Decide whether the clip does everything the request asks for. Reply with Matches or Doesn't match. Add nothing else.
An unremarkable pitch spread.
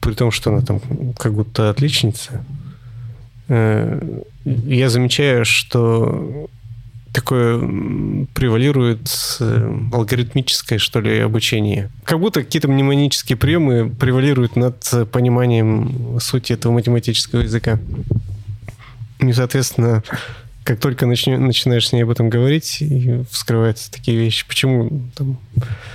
Doesn't match